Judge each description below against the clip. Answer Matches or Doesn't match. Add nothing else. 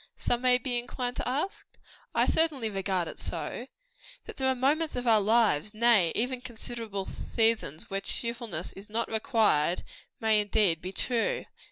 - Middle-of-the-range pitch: Doesn't match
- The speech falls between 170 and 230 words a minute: Doesn't match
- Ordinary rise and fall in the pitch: Matches